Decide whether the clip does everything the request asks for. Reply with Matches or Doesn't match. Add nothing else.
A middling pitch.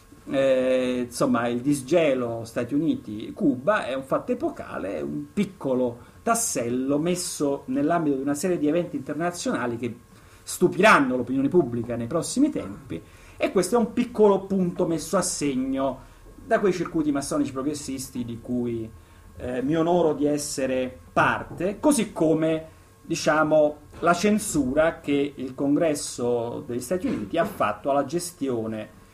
Matches